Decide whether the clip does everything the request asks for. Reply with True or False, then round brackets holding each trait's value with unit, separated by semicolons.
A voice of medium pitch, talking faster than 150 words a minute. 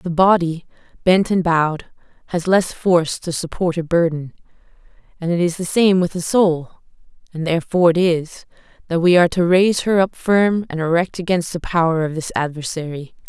True (170 Hz; 180 wpm)